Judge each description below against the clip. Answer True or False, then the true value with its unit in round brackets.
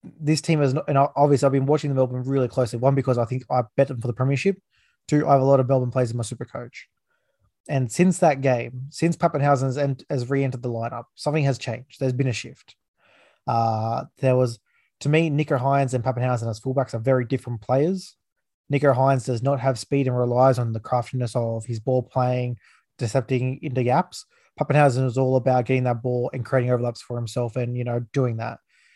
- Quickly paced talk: True (210 wpm)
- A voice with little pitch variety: True (2.3 semitones)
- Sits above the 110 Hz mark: True (130 Hz)